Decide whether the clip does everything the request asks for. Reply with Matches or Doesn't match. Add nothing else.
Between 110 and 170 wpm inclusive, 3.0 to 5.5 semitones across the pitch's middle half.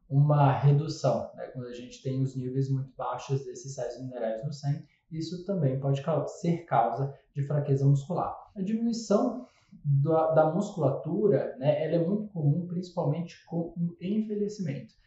Matches